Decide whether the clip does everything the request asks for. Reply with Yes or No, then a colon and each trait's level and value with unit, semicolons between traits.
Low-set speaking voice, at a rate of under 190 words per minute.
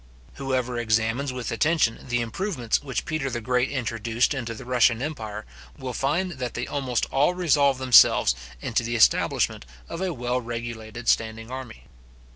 Yes: low, 125 Hz; average, 155 wpm